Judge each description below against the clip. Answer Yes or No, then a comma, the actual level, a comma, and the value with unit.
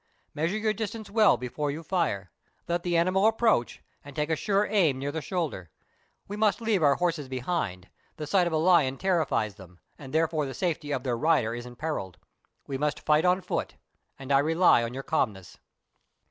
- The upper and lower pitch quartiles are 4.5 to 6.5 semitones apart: Yes, wide, 5.4 semitones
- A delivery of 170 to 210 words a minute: Yes, average, 190 wpm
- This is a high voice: No, medium, 155 Hz